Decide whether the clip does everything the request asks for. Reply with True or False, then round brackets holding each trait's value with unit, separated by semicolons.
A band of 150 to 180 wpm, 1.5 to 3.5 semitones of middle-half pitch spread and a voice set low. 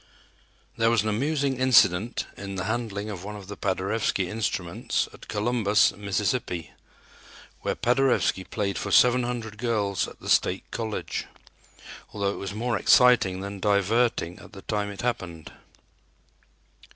False (140 wpm; 3.2 semitones; 105 Hz)